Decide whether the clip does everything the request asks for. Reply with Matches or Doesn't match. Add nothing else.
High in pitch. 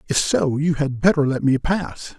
Doesn't match